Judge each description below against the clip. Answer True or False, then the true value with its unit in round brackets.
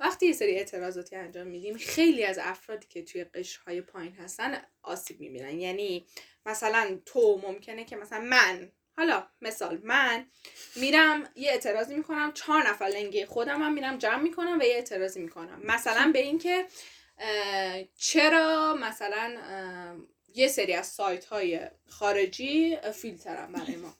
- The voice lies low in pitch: False (220 Hz)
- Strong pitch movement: True (7.9 semitones)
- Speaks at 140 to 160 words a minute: True (145 wpm)